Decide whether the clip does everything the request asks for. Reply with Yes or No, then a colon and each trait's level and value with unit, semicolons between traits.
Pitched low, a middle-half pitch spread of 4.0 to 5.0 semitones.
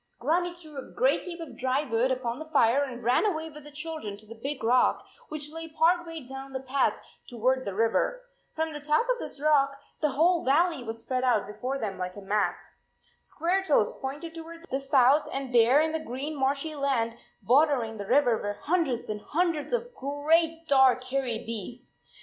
No: very high, 275 Hz; average, 4.5 semitones